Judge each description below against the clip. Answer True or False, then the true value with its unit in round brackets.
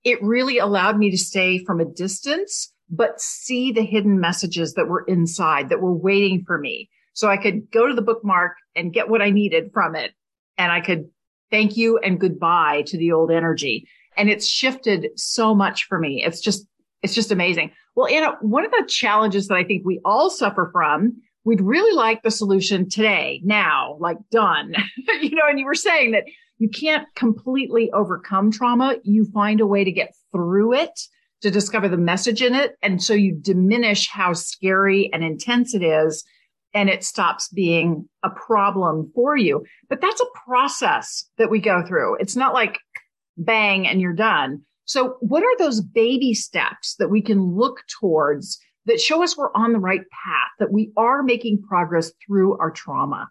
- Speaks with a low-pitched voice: False (210 Hz)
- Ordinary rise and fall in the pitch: True (4.2 semitones)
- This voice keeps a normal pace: True (190 wpm)